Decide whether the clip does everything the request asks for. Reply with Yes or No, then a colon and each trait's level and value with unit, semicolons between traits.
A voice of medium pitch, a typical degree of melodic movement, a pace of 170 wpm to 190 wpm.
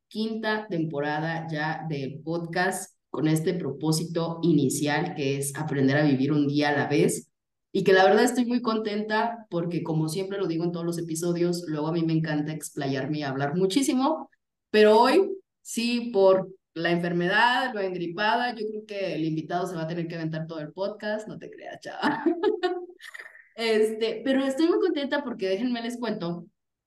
No: medium, 180 Hz; wide, 5.9 semitones; average, 175 wpm